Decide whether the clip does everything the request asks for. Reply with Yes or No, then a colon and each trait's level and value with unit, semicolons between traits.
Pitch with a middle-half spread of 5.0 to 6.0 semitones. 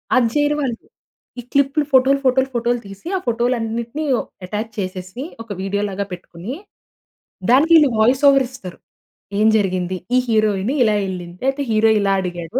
Yes: average, 5.3 semitones